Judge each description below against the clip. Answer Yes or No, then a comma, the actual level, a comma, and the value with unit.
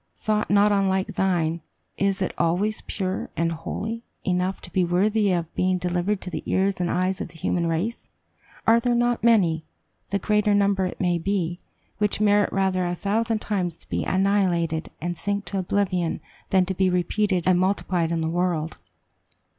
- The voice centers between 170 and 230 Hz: Yes, high, 190 Hz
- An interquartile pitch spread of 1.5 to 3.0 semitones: Yes, narrow, 2.5 semitones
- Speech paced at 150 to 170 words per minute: No, average, 180 wpm